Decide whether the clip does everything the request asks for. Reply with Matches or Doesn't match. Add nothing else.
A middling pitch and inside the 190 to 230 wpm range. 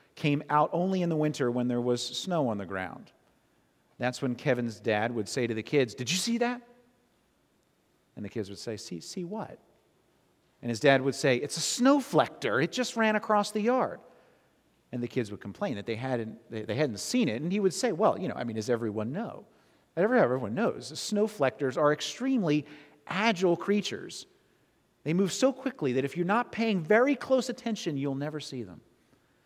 Matches